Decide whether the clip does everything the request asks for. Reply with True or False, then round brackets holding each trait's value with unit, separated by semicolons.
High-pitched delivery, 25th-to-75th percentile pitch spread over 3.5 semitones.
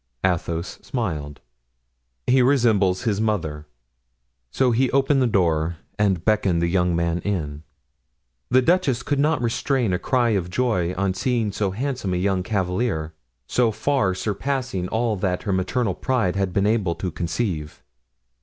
False (100 Hz; 5.5 semitones)